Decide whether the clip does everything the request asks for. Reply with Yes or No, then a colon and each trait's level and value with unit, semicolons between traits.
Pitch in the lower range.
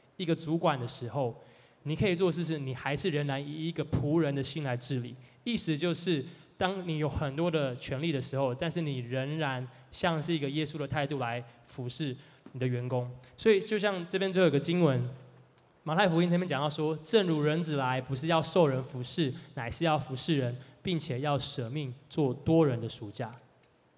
No: medium, 145 Hz